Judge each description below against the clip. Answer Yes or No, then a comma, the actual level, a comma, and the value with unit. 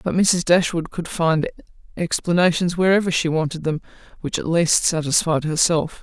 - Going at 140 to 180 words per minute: Yes, average, 150 wpm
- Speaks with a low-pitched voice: No, medium, 165 Hz